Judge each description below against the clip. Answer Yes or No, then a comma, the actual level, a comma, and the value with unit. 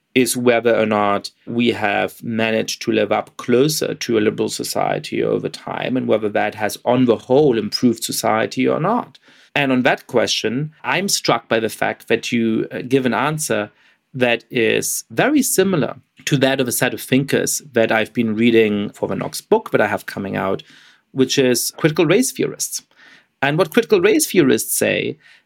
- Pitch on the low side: Yes, low, 125 Hz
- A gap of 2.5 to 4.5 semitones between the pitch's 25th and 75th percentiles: No, average, 5.0 semitones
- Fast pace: No, average, 180 wpm